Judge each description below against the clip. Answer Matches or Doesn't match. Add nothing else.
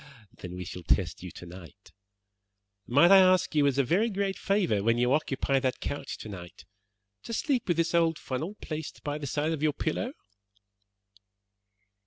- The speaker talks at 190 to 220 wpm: Doesn't match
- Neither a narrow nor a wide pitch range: Doesn't match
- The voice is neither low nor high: Matches